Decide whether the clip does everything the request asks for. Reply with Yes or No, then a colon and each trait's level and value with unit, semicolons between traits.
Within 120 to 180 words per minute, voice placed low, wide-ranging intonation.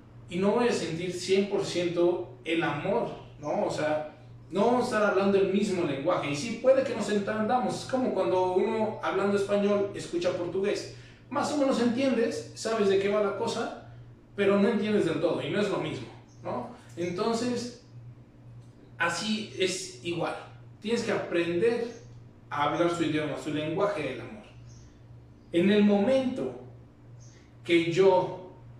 No: average, 155 wpm; medium, 180 Hz; wide, 6.1 semitones